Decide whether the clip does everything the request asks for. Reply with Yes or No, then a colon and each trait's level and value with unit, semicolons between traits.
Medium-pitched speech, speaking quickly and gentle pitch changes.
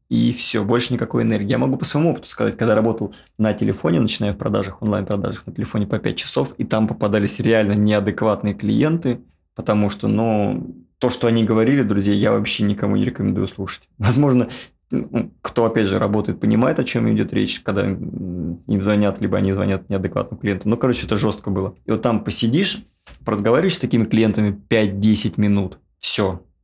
No: low, 105 Hz; fast, 175 wpm; narrow, 2.2 semitones